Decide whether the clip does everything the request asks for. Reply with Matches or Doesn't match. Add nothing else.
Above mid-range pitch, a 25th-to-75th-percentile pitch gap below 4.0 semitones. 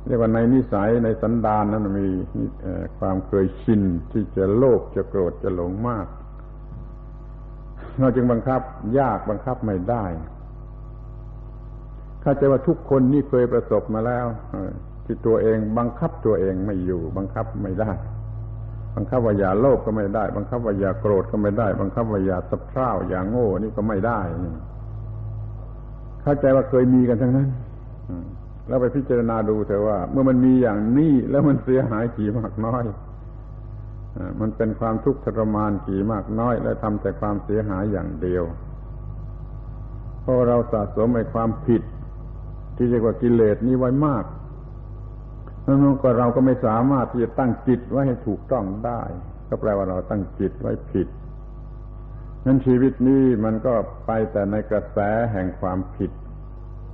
Doesn't match